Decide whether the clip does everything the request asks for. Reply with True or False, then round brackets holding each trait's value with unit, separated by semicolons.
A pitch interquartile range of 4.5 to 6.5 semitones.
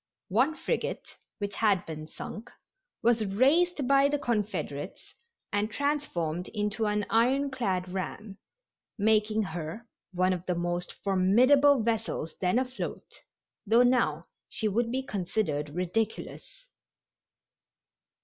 True (5.4 semitones)